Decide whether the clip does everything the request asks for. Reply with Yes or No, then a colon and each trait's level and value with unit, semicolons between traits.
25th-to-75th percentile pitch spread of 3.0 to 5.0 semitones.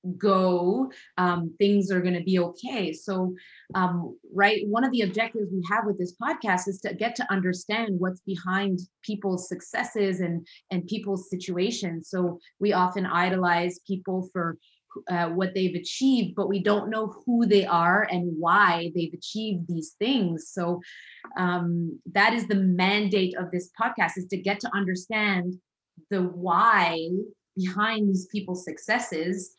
No: narrow, 2.4 semitones